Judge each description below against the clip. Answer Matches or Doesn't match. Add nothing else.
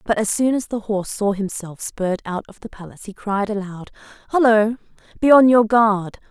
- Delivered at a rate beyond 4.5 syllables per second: Matches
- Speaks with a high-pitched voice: Matches